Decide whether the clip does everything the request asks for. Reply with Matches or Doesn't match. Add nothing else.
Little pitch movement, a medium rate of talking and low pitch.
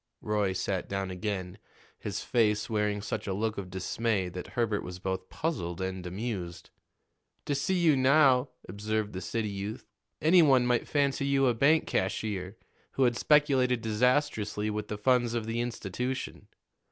Doesn't match